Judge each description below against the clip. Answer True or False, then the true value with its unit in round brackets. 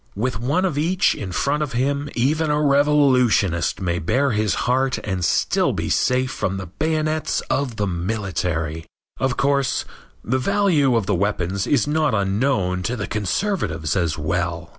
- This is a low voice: True (120 Hz)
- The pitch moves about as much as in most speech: False (7.3 semitones)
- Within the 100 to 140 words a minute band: False (160 wpm)